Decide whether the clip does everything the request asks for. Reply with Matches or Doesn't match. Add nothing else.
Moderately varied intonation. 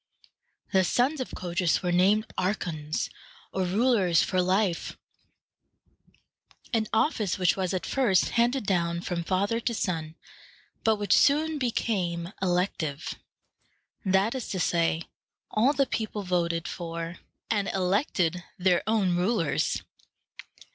Matches